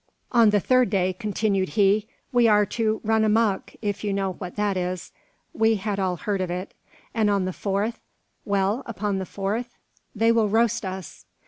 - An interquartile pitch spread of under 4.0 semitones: Yes, narrow, 2.5 semitones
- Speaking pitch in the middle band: No, high, 205 Hz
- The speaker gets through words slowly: No, average, 190 wpm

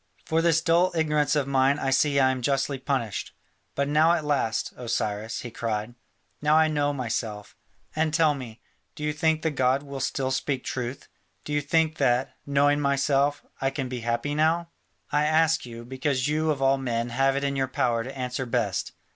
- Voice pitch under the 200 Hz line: Yes, medium, 140 Hz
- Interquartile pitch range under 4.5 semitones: Yes, average, 2.9 semitones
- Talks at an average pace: Yes, average, 195 wpm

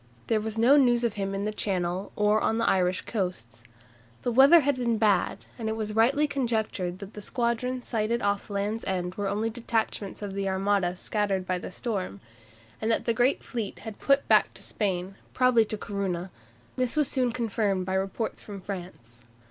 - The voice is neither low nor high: No, high, 210 Hz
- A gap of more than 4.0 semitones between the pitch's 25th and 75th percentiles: No, average, 3.4 semitones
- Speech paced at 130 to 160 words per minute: No, average, 190 wpm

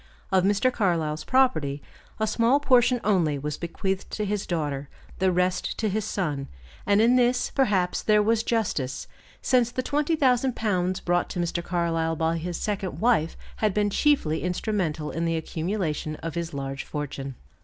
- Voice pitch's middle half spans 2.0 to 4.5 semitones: No, wide, 5.5 semitones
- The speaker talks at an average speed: Yes, average, 165 wpm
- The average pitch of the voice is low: No, medium, 185 Hz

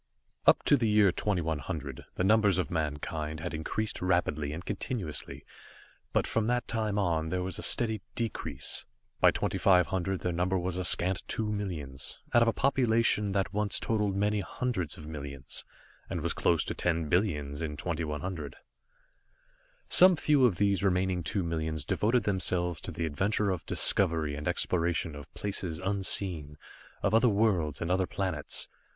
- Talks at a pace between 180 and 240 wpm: No, average, 160 wpm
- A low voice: Yes, very low, 90 Hz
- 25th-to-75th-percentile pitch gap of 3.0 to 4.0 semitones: No, average, 4.5 semitones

